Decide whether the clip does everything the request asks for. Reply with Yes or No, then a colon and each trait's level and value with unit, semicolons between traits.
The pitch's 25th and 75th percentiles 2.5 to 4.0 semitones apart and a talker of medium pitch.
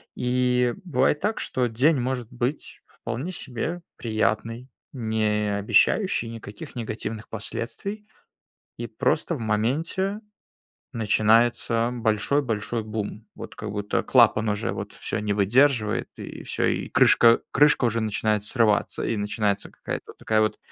No: average, 3.0 semitones; low, 115 Hz